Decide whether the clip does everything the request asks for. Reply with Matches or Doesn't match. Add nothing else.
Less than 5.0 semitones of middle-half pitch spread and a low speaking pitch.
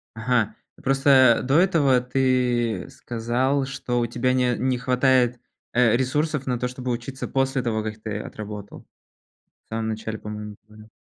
Matches